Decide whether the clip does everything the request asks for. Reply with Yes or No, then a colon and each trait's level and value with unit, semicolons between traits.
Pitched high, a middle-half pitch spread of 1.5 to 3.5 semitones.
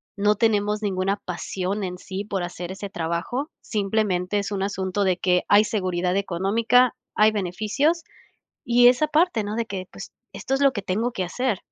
Yes: high, 205 Hz; average, 3.2 semitones